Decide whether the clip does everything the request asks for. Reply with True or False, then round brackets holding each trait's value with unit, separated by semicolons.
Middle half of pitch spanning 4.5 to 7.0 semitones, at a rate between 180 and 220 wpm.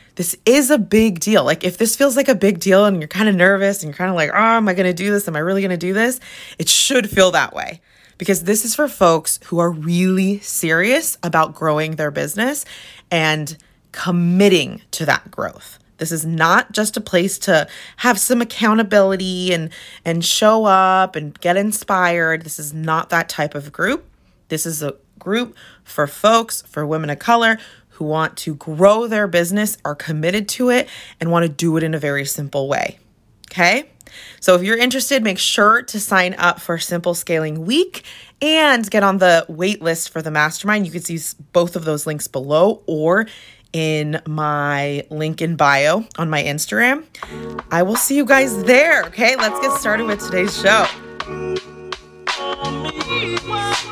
True (5.2 semitones; 185 wpm)